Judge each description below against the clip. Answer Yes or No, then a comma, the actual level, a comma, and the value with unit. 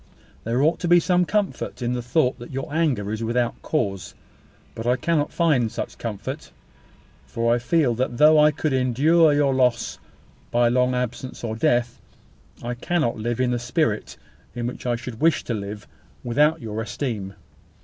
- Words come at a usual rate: Yes, average, 175 wpm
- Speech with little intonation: No, average, 4.3 semitones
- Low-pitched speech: Yes, low, 125 Hz